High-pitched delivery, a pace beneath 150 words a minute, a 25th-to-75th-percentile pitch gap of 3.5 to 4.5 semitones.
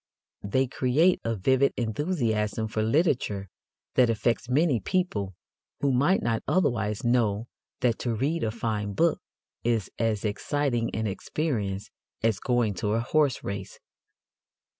No: low, 115 Hz; slow, 135 wpm; average, 4.2 semitones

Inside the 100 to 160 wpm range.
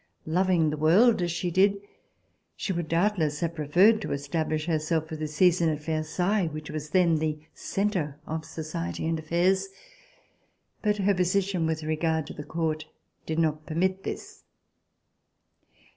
Yes: average, 150 wpm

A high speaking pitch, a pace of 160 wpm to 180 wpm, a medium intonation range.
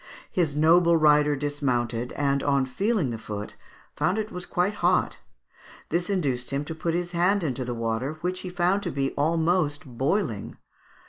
No: medium, 150 Hz; average, 170 wpm; average, 4.9 semitones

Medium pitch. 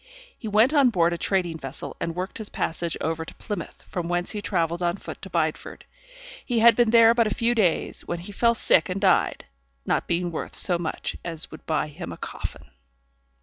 Yes: medium, 180 Hz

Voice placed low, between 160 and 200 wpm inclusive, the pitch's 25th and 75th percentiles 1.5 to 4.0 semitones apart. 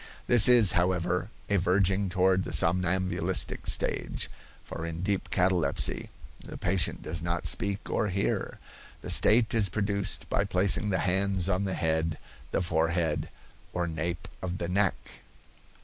No: very low, 90 Hz; average, 145 wpm; narrow, 2.4 semitones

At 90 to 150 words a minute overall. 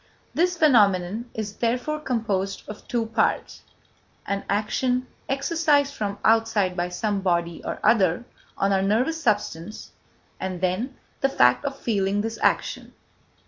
Yes: slow, 135 wpm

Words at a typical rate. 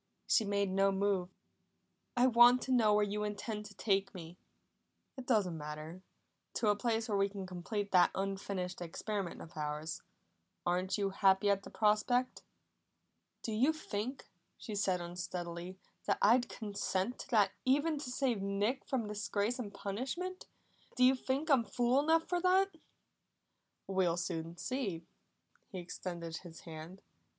Yes: average, 150 wpm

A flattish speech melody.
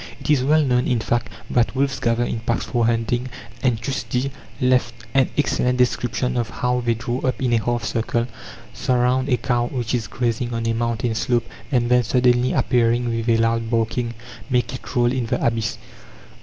Yes: narrow, 1.4 semitones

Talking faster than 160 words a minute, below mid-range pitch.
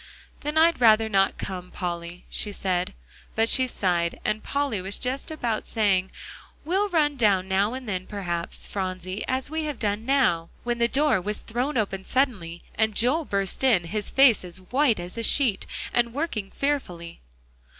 No: average, 170 wpm; high, 215 Hz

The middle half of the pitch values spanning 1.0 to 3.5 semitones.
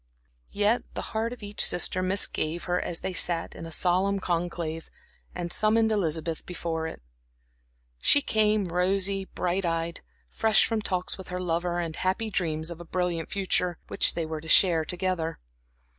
Yes: average, 2.9 semitones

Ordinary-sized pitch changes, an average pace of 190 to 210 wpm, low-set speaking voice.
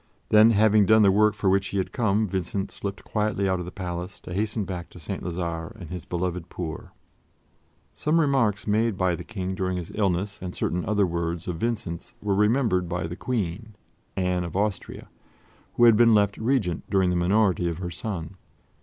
Yes: average, 3.3 semitones; average, 195 wpm; very low, 95 Hz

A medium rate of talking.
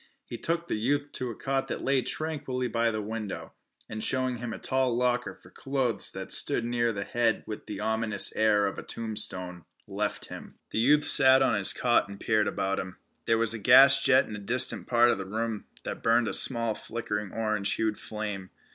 No: fast, 210 wpm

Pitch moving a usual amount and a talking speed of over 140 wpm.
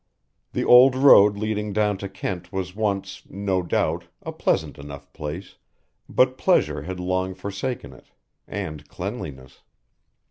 No: average, 3.0 semitones; slow, 135 wpm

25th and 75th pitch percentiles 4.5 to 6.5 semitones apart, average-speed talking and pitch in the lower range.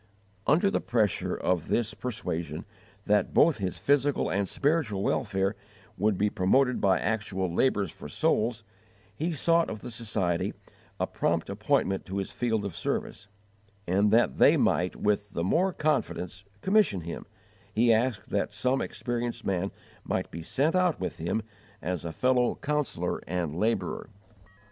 Yes: average, 5.1 semitones; average, 150 wpm; low, 105 Hz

